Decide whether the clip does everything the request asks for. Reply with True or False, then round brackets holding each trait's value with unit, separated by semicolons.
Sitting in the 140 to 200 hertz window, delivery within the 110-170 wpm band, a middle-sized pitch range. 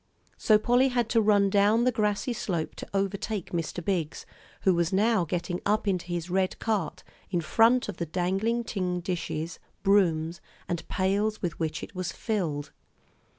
True (190 Hz; 165 wpm; 3.7 semitones)